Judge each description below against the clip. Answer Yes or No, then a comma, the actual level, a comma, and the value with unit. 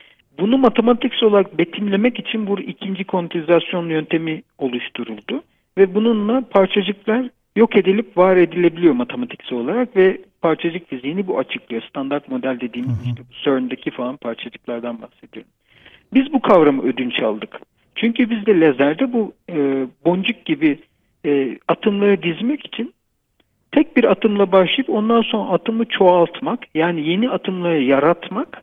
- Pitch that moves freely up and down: Yes, wide, 7.2 semitones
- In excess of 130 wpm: No, average, 125 wpm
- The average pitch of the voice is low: No, high, 190 Hz